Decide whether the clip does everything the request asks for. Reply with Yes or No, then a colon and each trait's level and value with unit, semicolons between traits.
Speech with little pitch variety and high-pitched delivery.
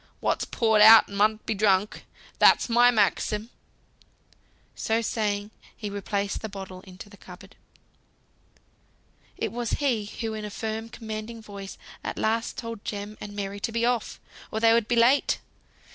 Yes: narrow, 2.0 semitones; high, 215 Hz